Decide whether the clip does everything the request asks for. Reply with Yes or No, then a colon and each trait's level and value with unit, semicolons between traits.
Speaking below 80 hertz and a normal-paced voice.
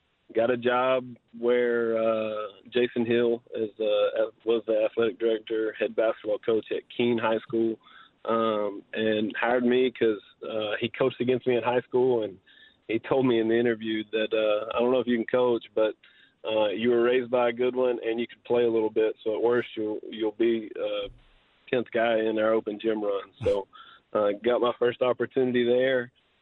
No: low, 120 Hz; average, 195 wpm